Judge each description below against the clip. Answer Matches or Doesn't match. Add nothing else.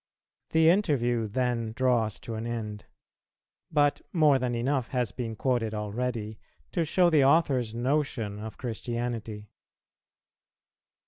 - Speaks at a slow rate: Matches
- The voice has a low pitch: Matches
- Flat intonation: Doesn't match